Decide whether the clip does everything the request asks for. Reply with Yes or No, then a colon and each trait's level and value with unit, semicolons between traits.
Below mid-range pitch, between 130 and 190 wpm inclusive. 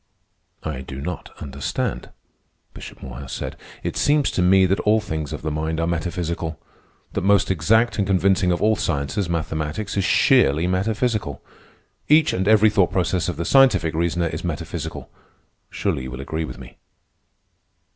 Yes: very low, 85 Hz; average, 160 wpm